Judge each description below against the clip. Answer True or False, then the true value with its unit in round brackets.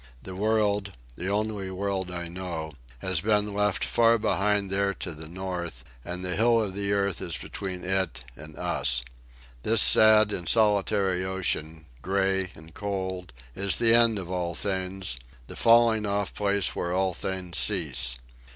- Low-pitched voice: True (95 Hz)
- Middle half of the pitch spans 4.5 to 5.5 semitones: False (2.8 semitones)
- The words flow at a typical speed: True (150 wpm)